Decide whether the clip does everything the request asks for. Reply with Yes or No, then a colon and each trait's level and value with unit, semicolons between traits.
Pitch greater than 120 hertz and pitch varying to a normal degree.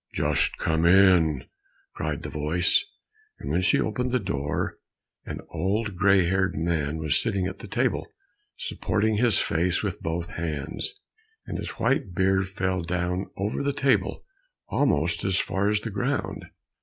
No: very low, 95 Hz; average, 3.5 semitones